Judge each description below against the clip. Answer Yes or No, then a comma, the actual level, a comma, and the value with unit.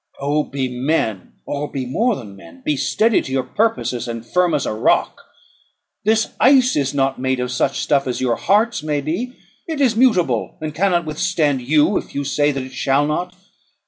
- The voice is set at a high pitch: No, medium, 145 Hz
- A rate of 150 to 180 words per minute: No, average, 195 wpm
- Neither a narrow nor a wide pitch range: No, wide, 5.8 semitones